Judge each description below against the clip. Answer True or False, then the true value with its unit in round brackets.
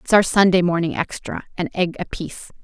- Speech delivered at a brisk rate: False (160 wpm)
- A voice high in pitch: False (180 Hz)